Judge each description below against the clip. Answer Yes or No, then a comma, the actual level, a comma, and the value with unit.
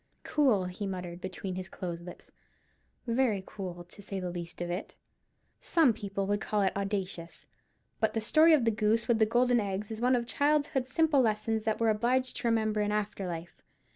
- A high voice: Yes, high, 210 Hz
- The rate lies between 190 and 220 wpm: Yes, average, 195 wpm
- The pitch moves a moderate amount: Yes, average, 4.0 semitones